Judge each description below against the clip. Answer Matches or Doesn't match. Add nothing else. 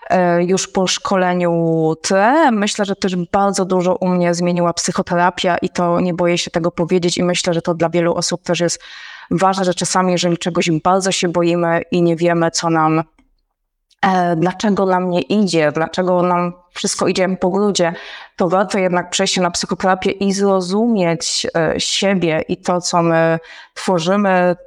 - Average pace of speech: Doesn't match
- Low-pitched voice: Doesn't match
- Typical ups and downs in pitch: Doesn't match